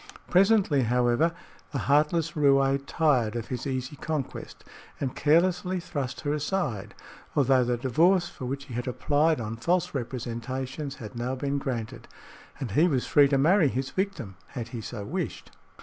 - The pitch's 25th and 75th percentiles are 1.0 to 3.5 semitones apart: No, average, 4.0 semitones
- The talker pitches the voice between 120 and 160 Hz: Yes, low, 135 Hz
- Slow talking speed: No, average, 160 wpm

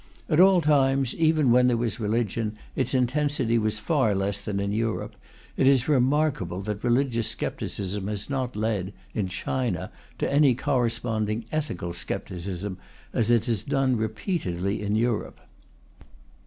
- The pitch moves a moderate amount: Yes, average, 4.4 semitones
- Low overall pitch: Yes, low, 115 Hz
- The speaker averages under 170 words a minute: Yes, average, 140 wpm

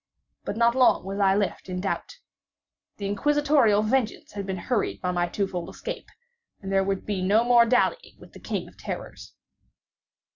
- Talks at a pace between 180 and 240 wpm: Yes, average, 185 wpm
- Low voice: No, high, 205 Hz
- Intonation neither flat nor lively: Yes, average, 4.0 semitones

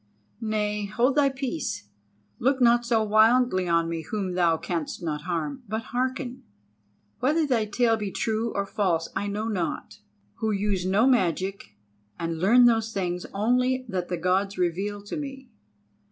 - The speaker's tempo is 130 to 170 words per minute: Yes, average, 155 wpm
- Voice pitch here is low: No, high, 210 Hz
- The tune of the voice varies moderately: Yes, average, 5.0 semitones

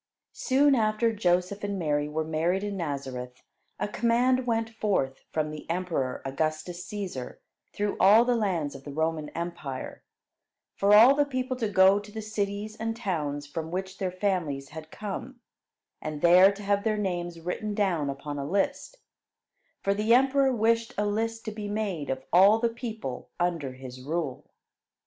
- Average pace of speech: Yes, average, 170 wpm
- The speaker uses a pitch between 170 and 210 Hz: Yes, high, 190 Hz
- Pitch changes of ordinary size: No, wide, 5.7 semitones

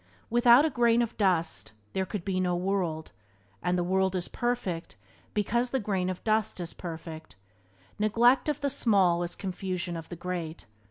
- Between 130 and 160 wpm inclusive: No, average, 170 wpm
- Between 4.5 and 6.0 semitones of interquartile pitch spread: Yes, average, 4.9 semitones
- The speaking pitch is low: No, high, 190 Hz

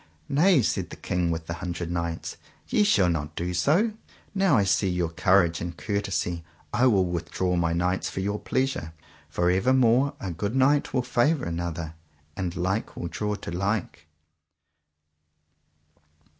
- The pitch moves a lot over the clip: Yes, wide, 5.7 semitones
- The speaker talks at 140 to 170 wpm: Yes, average, 155 wpm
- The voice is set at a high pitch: No, very low, 95 Hz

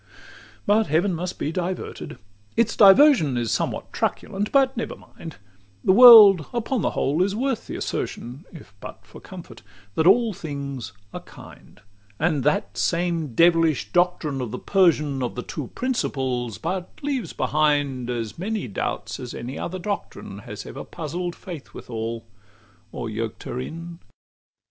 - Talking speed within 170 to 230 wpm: No, average, 155 wpm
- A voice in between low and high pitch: Yes, medium, 165 Hz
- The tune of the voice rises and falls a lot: Yes, wide, 6.6 semitones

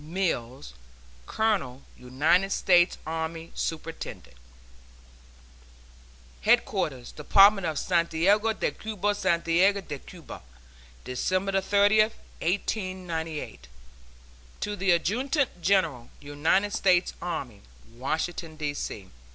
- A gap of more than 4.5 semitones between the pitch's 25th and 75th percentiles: No, average, 4.2 semitones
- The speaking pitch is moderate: Yes, medium, 175 Hz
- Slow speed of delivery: Yes, slow, 85 wpm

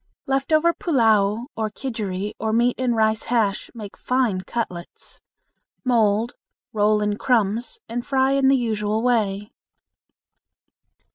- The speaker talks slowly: Yes, slow, 125 wpm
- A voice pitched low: No, high, 225 Hz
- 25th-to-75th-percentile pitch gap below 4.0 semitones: Yes, average, 3.1 semitones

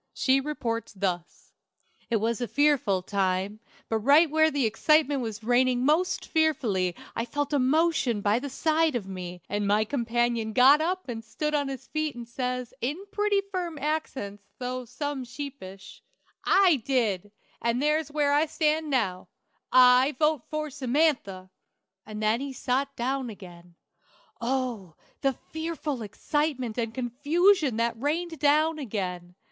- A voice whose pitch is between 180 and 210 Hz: No, very high, 255 Hz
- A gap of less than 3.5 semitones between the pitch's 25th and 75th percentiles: No, average, 5.2 semitones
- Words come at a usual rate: Yes, average, 150 wpm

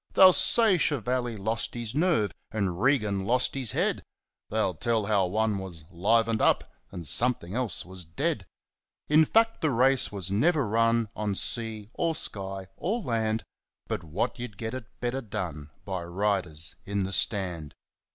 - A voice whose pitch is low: Yes, low, 110 Hz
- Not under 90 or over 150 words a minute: No, average, 160 wpm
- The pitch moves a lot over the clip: No, average, 4.7 semitones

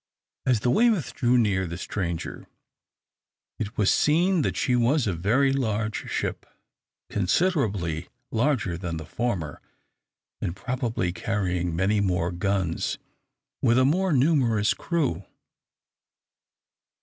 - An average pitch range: No, wide, 6.5 semitones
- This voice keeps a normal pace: No, slow, 115 wpm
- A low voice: Yes, low, 110 Hz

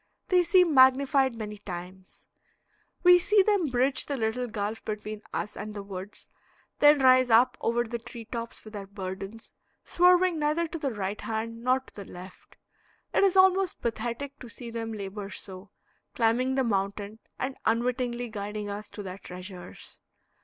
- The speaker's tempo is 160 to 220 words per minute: Yes, average, 165 wpm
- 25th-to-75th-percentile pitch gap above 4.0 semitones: Yes, average, 4.4 semitones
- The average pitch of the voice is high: Yes, high, 230 Hz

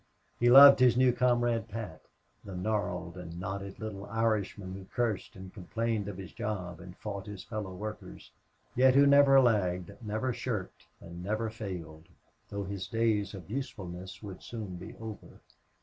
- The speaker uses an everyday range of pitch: Yes, average, 3.6 semitones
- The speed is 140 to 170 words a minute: Yes, average, 160 wpm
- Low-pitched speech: Yes, low, 105 Hz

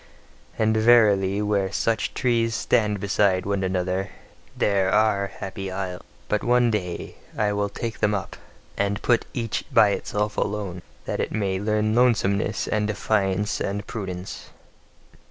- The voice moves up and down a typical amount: No, narrow, 1.9 semitones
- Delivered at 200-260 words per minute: No, average, 140 wpm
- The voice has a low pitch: Yes, low, 105 Hz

